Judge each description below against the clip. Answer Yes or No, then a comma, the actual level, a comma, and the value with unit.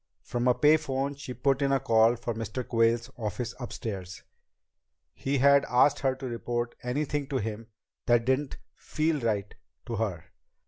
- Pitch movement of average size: Yes, average, 3.1 semitones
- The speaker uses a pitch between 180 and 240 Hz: No, low, 125 Hz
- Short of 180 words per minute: Yes, average, 165 wpm